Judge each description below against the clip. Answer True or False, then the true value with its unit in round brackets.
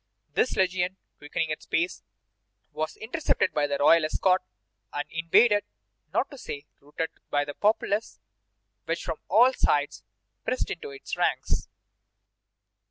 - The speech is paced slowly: True (130 wpm)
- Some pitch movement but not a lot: False (5.8 semitones)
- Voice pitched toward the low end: False (170 Hz)